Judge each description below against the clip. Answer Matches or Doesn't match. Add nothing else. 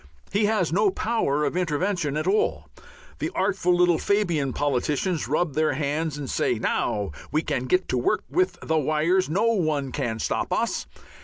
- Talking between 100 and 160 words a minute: Doesn't match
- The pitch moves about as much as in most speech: Matches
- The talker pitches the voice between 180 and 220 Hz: Doesn't match